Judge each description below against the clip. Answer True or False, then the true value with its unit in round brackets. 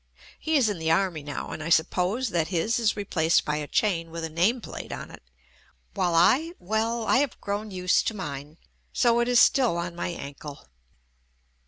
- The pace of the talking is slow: False (205 wpm)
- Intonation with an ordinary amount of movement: False (5.7 semitones)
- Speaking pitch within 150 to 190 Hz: True (185 Hz)